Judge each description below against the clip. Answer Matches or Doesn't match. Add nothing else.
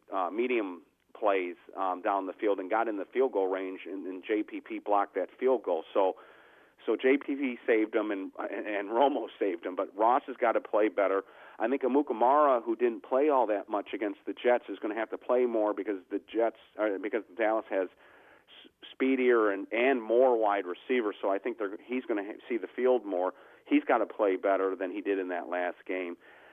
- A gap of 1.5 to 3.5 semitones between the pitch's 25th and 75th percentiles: Doesn't match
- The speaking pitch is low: Matches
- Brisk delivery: Matches